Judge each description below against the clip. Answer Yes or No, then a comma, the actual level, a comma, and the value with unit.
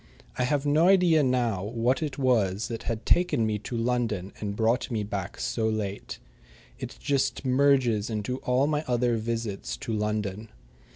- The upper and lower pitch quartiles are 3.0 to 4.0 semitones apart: Yes, average, 3.4 semitones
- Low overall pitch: Yes, low, 115 Hz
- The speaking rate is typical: Yes, average, 165 wpm